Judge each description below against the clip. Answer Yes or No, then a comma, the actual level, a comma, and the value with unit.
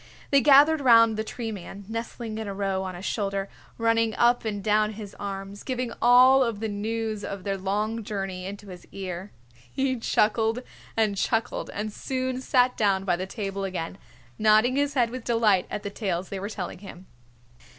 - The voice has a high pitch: Yes, high, 215 Hz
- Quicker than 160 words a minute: Yes, average, 185 wpm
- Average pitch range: Yes, average, 3.0 semitones